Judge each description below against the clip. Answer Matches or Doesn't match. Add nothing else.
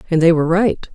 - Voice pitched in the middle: Matches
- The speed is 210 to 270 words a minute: Matches